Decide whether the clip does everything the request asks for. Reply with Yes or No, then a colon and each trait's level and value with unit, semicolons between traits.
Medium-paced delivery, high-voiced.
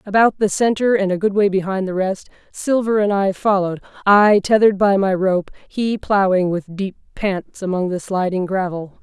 Yes: average, 180 wpm; high, 195 Hz